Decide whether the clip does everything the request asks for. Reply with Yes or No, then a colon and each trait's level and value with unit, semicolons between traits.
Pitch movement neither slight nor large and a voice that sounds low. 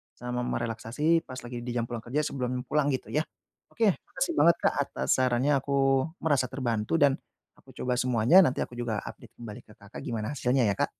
Yes: average, 3.2 semitones; low, 125 Hz